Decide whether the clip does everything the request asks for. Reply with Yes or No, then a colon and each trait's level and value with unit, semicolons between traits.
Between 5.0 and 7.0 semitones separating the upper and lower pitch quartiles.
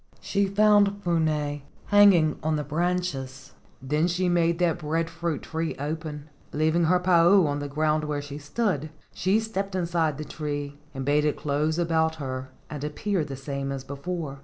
No: average, 3.3 semitones